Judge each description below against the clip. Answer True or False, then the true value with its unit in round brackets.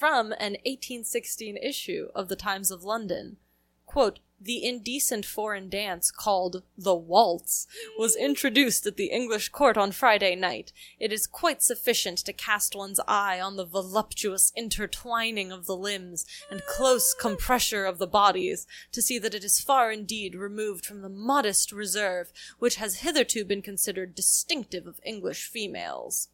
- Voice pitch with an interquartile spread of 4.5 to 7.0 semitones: False (3.9 semitones)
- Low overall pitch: False (210 Hz)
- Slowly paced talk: False (155 wpm)